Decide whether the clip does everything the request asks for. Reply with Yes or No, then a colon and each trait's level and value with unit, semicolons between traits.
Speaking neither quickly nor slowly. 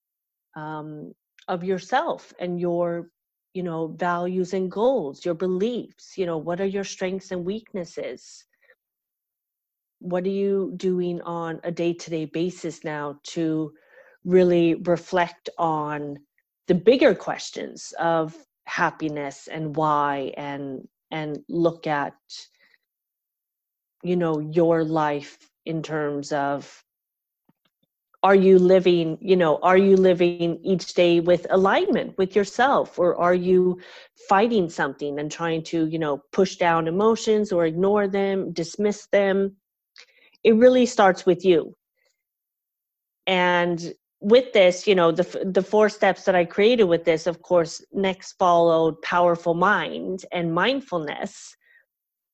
No: slow, 125 wpm